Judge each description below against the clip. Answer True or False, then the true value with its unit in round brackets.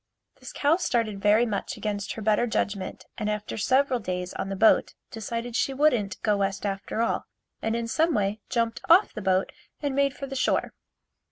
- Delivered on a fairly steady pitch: False (4.2 semitones)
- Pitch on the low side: False (220 Hz)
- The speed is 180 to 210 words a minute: True (190 wpm)